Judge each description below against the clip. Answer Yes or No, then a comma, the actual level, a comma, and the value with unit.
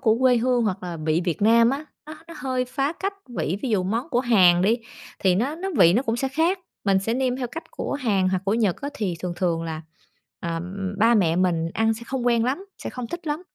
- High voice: Yes, high, 225 Hz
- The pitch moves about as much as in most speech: No, wide, 5.9 semitones